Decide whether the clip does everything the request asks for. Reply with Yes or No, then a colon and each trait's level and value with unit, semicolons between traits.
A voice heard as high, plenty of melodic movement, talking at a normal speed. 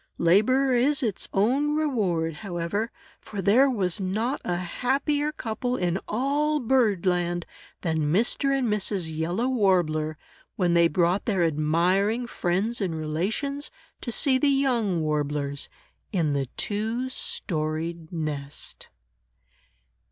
No: high, 195 Hz; wide, 6.8 semitones; slow, 120 wpm